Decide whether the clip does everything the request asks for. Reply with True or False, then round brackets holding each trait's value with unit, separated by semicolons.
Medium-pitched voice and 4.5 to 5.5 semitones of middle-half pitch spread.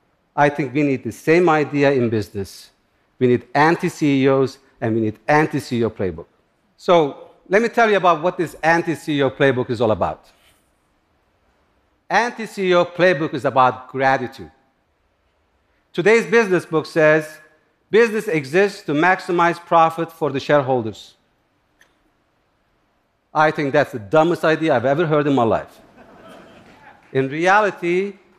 True (150 Hz; 5.2 semitones)